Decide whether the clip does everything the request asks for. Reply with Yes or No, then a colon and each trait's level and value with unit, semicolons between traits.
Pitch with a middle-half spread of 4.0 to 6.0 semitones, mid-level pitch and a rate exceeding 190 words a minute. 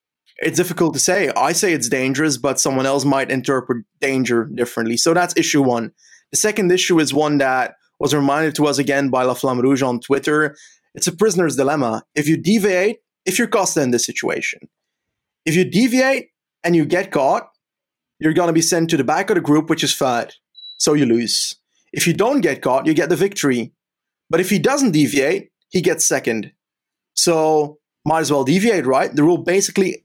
Yes: average, 4.5 semitones; medium, 155 Hz; average, 200 wpm